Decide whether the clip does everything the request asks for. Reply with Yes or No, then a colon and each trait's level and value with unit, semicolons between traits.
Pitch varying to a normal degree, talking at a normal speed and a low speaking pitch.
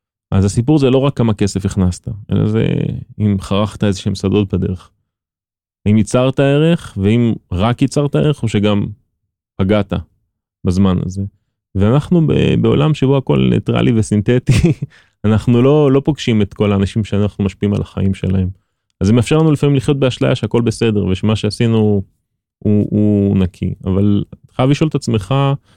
No: average, 4.3 semitones; fast, 155 wpm; low, 105 Hz